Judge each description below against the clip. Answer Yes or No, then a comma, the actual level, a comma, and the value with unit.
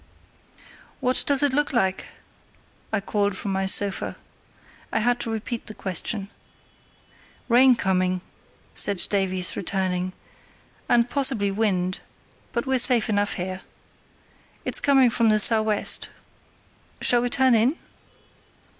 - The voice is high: Yes, high, 215 Hz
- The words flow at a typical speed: No, slow, 125 wpm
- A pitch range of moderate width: Yes, average, 4.2 semitones